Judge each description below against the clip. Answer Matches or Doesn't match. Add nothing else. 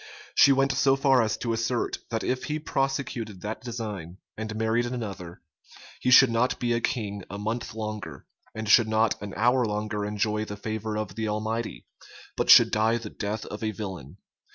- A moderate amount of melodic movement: Doesn't match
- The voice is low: Matches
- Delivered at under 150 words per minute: Doesn't match